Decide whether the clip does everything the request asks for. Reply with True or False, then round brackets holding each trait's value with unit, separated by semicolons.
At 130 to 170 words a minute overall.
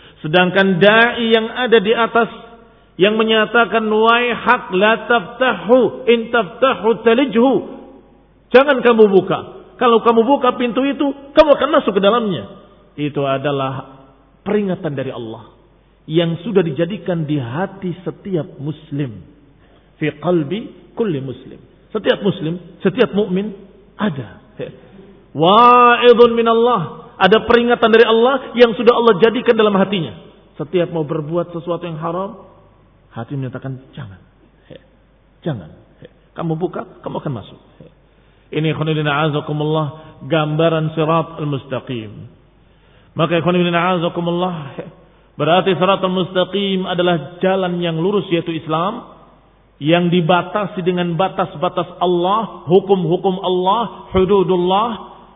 False (115 wpm)